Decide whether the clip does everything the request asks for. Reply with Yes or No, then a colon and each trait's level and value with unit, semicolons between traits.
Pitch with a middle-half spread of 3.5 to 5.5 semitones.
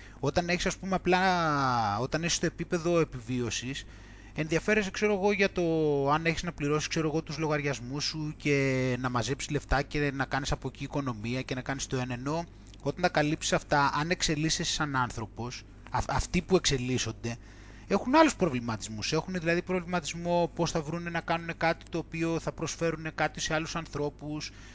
Yes: average, 4.6 semitones